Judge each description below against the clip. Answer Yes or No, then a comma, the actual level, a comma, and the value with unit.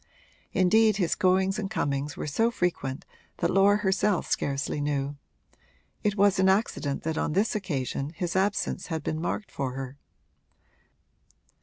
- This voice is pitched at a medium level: Yes, medium, 180 Hz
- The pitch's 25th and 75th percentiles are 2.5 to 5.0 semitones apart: No, wide, 5.6 semitones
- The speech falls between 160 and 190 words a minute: No, average, 145 wpm